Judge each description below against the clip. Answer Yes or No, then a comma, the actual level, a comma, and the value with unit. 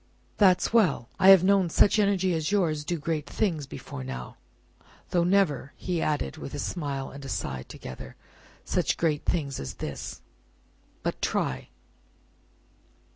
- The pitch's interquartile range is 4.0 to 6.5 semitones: Yes, average, 5.2 semitones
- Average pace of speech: Yes, average, 145 wpm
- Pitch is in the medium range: Yes, medium, 160 Hz